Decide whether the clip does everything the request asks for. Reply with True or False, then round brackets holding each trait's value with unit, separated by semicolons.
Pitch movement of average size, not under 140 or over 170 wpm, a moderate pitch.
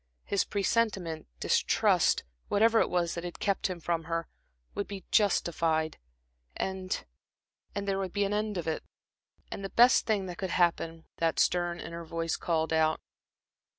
True (3.2 semitones; 160 wpm; 175 Hz)